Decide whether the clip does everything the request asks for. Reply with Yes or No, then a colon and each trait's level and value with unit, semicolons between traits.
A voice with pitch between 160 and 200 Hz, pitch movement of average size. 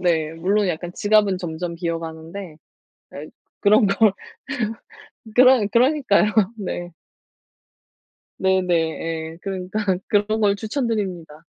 Yes: high, 190 Hz; average, 4.1 semitones